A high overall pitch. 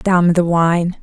No: medium, 175 Hz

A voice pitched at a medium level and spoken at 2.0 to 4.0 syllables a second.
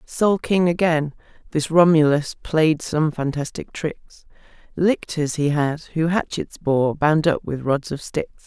Yes: medium, 155 Hz; 3.8 syllables/s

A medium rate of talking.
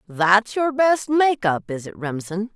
Yes: average, 165 wpm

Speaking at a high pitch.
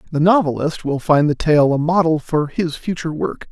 No: medium, 155 Hz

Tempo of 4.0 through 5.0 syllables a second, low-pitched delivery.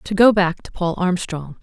No: 4.5 syllables/s; medium, 180 Hz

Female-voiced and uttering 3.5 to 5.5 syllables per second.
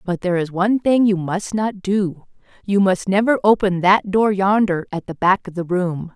Yes: female; 4.9 syllables/s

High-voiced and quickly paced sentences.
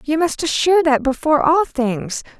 No: very high, 295 Hz; average, 175 wpm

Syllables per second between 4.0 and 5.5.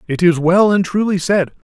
Yes: 5.0 syllables/s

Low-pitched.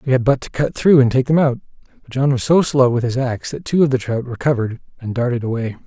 Yes: low, 130 Hz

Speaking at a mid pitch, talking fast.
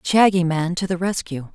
No: medium, 175 Hz; average, 195 wpm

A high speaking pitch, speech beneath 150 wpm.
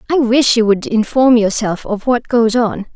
No: high, 230 Hz; fast, 205 wpm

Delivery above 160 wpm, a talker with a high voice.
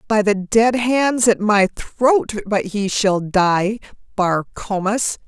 No: average, 150 wpm; high, 205 Hz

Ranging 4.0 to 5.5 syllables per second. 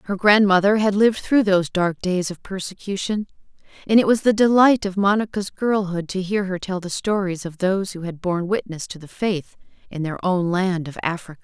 Yes: 5.4 syllables/s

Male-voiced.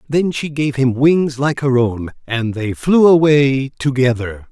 Yes: male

